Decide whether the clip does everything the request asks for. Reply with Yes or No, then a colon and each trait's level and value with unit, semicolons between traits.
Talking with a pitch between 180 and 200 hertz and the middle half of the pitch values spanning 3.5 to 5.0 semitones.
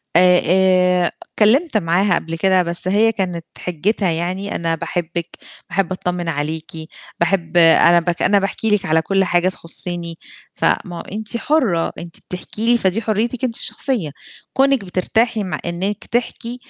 Yes: medium, 185 Hz; average, 3.8 semitones